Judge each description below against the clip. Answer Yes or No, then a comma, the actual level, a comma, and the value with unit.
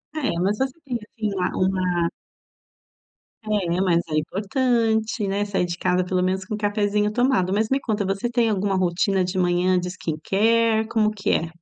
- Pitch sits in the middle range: No, high, 200 Hz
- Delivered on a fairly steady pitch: No, average, 3.2 semitones